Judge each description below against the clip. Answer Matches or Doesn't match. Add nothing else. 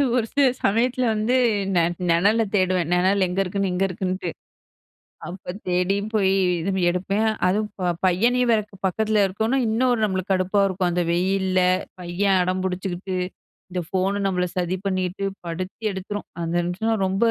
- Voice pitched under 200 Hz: Matches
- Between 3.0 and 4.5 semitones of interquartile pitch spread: Doesn't match